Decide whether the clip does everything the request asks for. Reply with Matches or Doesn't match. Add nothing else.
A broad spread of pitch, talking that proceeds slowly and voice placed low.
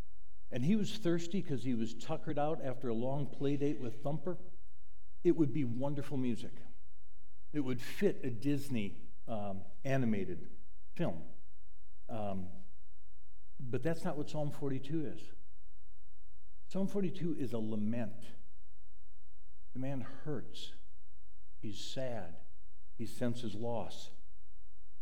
Matches